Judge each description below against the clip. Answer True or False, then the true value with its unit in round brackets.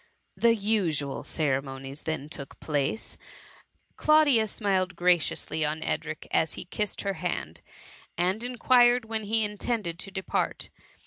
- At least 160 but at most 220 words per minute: False (135 wpm)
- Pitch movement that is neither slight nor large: False (6.0 semitones)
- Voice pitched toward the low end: False (185 Hz)